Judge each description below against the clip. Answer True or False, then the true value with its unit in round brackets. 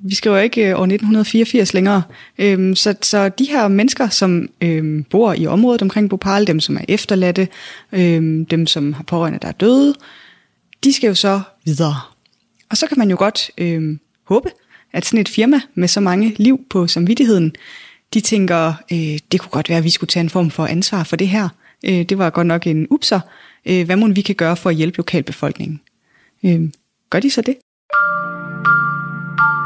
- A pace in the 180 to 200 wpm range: True (190 wpm)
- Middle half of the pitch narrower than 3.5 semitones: False (4.4 semitones)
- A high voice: True (195 Hz)